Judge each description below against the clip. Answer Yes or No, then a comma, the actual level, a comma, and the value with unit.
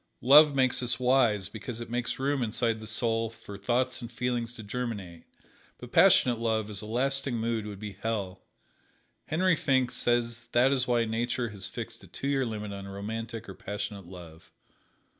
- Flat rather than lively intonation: No, average, 3.0 semitones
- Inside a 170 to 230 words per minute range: Yes, average, 180 wpm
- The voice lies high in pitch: No, low, 115 Hz